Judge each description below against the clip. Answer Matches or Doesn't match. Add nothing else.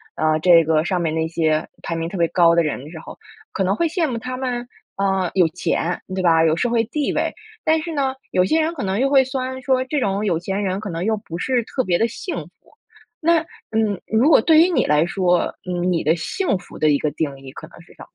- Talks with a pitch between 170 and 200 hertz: Matches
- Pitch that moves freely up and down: Matches